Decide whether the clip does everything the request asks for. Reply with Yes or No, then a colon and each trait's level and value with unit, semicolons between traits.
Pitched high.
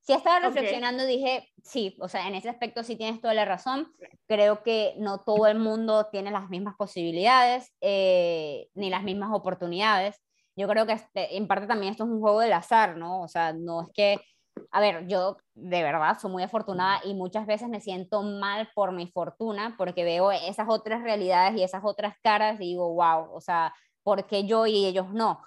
Yes: high, 205 Hz